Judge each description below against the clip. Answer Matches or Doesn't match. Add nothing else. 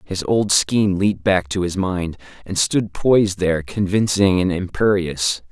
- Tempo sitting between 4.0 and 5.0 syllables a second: Matches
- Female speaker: Doesn't match